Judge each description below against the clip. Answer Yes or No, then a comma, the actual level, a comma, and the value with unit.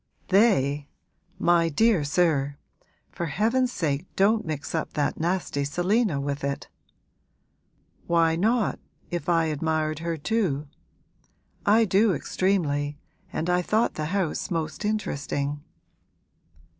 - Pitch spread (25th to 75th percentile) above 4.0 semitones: Yes, average, 5.2 semitones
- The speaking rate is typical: No, slow, 115 wpm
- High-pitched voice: No, medium, 165 Hz